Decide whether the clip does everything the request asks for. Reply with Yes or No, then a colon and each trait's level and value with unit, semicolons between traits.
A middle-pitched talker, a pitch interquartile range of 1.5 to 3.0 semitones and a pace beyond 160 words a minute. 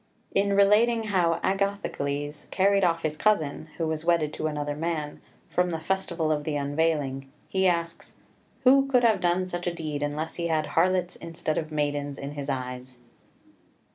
No: medium, 165 Hz; average, 4.1 semitones; average, 170 wpm